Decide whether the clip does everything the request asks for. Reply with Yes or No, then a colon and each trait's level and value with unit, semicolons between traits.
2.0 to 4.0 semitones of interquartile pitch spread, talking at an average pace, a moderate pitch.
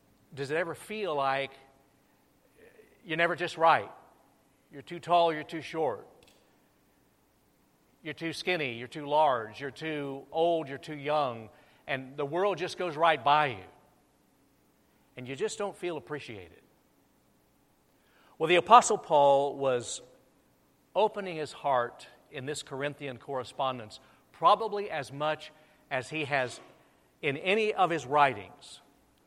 No: average, 3.5 semitones; slow, 130 wpm; medium, 150 Hz